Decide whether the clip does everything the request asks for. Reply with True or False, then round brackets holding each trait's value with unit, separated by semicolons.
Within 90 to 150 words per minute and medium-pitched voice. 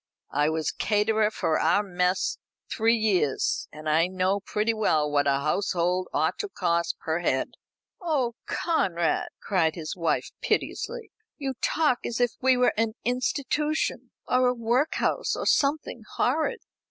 False (145 wpm; 210 Hz)